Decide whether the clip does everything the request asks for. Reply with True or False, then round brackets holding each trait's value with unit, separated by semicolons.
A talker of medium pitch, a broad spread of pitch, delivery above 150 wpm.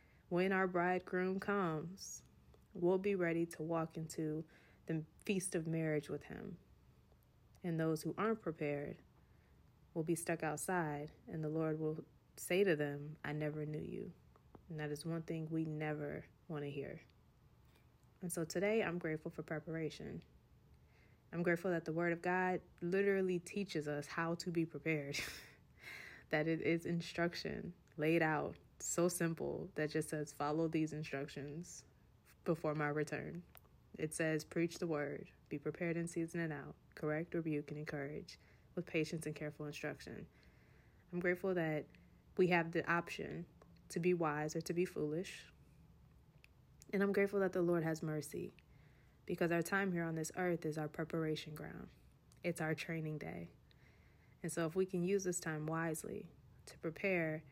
False (165 Hz; 2.5 semitones; 160 wpm)